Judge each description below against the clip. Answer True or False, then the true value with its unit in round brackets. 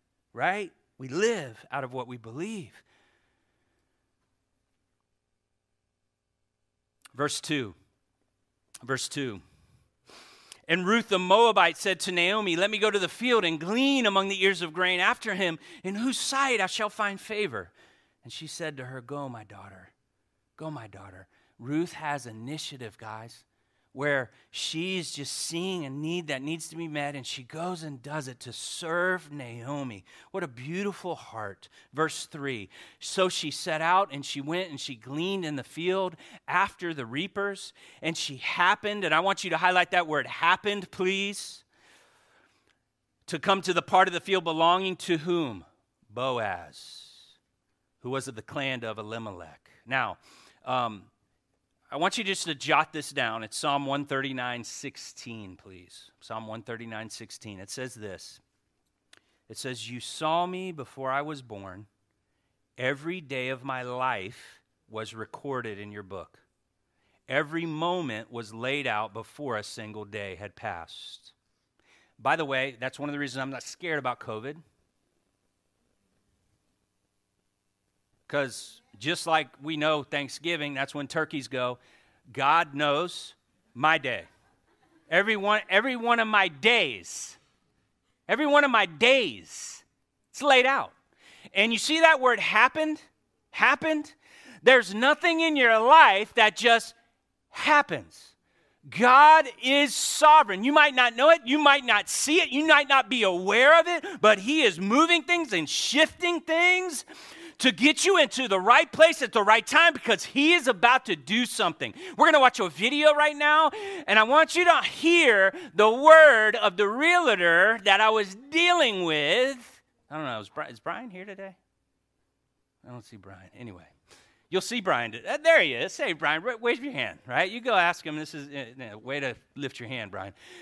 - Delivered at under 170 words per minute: True (160 wpm)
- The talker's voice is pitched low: False (165 Hz)